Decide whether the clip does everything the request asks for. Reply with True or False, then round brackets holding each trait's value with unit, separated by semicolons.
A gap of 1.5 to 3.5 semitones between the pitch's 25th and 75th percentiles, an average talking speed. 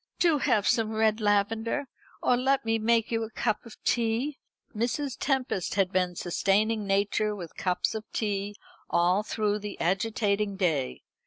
True (2.5 semitones; 155 wpm)